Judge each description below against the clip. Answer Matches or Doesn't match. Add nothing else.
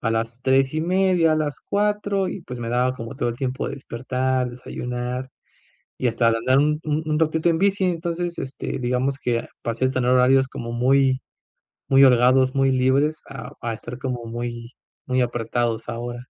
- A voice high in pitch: Doesn't match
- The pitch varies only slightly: Doesn't match